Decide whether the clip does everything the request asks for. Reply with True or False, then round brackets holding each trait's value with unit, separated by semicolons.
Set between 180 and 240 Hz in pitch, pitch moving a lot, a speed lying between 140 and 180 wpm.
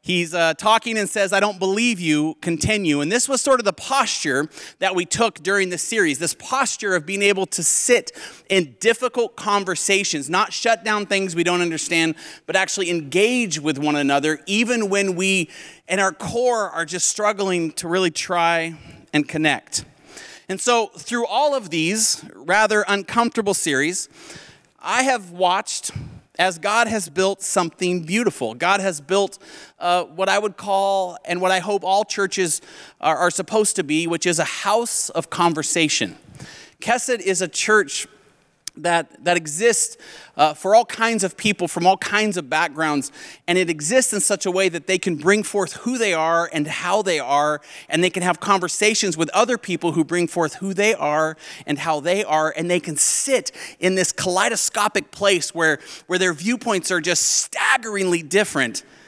False (185 Hz; 3.7 semitones; 175 wpm)